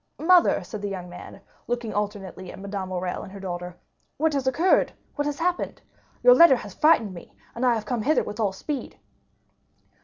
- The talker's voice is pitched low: No, high, 215 Hz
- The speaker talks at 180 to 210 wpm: Yes, average, 185 wpm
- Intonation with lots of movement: Yes, wide, 7.3 semitones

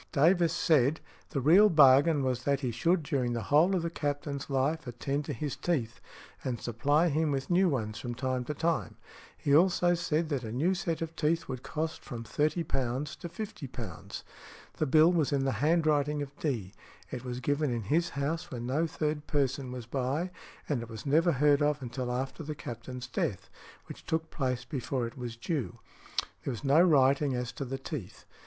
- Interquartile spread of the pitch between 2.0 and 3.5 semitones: No, average, 4.0 semitones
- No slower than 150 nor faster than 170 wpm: No, average, 190 wpm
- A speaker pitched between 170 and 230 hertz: No, medium, 140 Hz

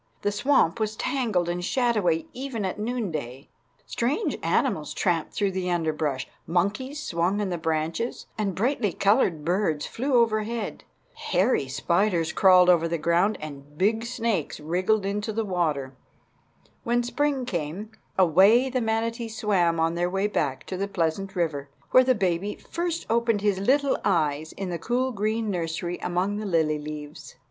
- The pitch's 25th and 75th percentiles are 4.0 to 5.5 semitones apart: Yes, average, 5.2 semitones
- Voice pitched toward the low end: No, high, 195 Hz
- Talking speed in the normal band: Yes, average, 155 wpm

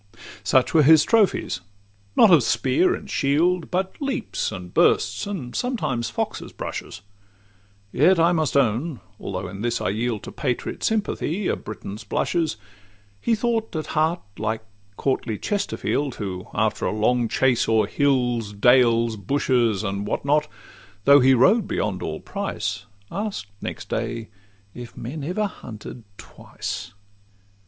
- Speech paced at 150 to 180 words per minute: No, slow, 135 wpm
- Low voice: Yes, low, 125 Hz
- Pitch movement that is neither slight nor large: No, wide, 7.4 semitones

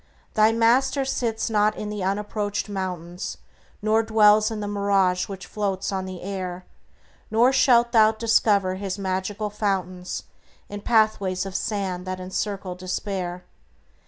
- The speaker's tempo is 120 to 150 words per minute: Yes, slow, 135 wpm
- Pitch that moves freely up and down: No, narrow, 2.6 semitones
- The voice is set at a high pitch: Yes, high, 200 Hz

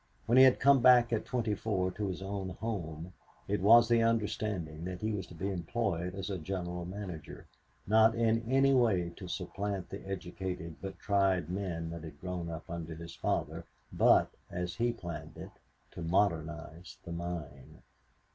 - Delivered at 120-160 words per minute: No, average, 175 wpm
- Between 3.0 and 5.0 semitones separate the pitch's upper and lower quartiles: Yes, average, 4.1 semitones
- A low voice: Yes, very low, 95 Hz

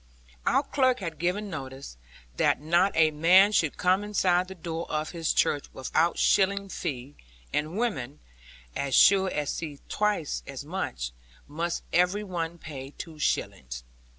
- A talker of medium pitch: Yes, medium, 165 Hz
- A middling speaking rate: Yes, average, 150 wpm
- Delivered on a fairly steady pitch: No, average, 4.5 semitones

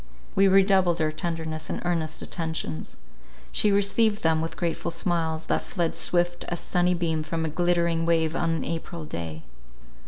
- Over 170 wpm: No, average, 160 wpm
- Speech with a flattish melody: Yes, narrow, 1.6 semitones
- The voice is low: No, medium, 165 Hz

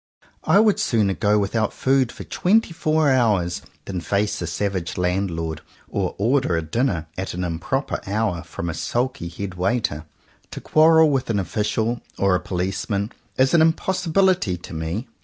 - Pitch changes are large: Yes, wide, 6.8 semitones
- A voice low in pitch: Yes, low, 105 Hz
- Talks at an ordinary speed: Yes, average, 160 wpm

